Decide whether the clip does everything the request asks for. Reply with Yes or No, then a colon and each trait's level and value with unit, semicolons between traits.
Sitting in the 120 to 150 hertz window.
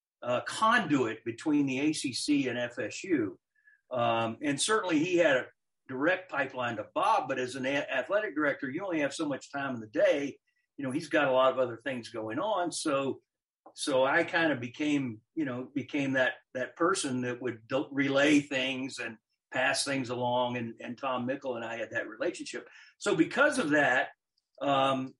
Yes: medium, 140 Hz